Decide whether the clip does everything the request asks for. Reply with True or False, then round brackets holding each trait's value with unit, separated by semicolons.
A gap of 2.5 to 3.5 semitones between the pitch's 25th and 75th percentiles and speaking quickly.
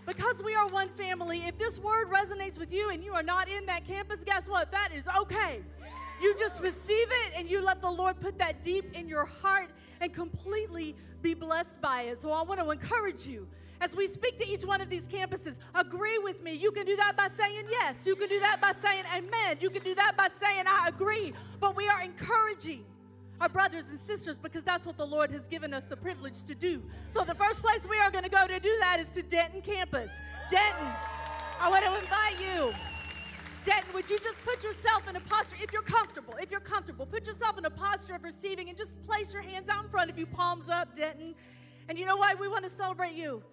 True (2.8 semitones; 230 wpm)